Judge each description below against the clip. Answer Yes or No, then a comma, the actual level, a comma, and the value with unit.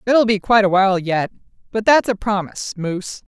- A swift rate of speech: No, average, 195 wpm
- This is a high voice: Yes, high, 205 Hz